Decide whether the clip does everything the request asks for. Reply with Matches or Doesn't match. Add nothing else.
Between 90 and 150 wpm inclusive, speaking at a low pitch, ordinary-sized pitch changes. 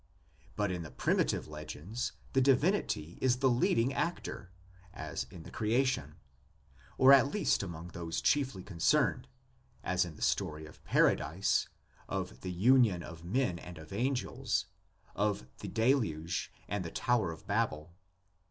Doesn't match